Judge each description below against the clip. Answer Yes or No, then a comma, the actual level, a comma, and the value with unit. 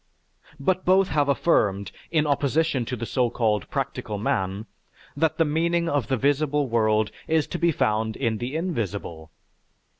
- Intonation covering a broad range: Yes, wide, 6.6 semitones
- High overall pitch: No, low, 135 Hz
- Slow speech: No, average, 155 wpm